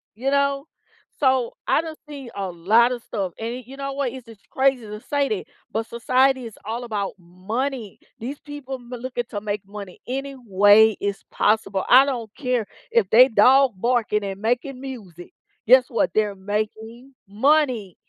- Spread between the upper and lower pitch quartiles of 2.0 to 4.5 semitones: Yes, average, 4.2 semitones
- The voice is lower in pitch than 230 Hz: No, high, 235 Hz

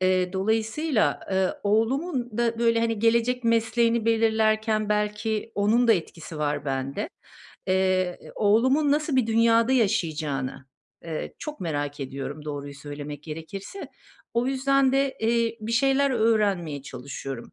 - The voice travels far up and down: Yes, wide, 6.3 semitones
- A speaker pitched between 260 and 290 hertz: No, high, 220 Hz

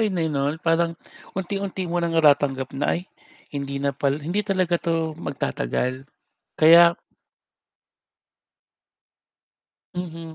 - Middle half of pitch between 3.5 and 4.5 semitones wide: Yes, average, 3.8 semitones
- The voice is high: No, medium, 165 Hz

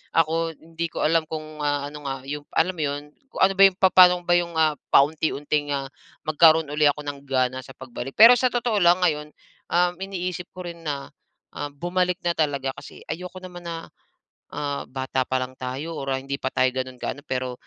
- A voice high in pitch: No, medium, 150 Hz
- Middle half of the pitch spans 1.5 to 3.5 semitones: No, average, 4.0 semitones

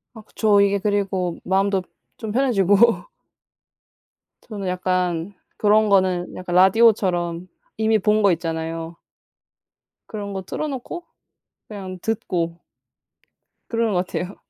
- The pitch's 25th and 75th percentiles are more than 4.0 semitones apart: No, average, 3.1 semitones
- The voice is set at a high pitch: Yes, high, 195 Hz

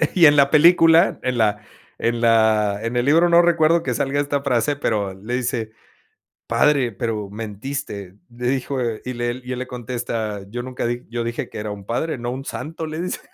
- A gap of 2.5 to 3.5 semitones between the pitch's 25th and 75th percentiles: No, average, 4.3 semitones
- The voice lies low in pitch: Yes, low, 125 Hz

